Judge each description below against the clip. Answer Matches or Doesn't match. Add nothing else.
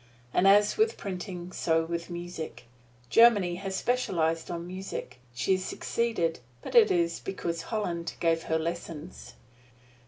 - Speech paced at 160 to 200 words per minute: Doesn't match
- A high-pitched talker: Doesn't match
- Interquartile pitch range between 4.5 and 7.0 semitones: Doesn't match